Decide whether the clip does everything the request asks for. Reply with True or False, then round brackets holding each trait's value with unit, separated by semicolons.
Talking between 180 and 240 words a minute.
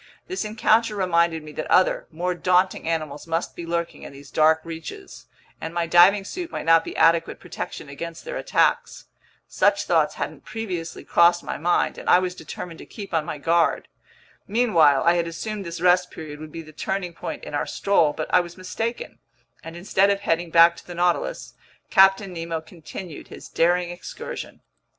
True (185 wpm)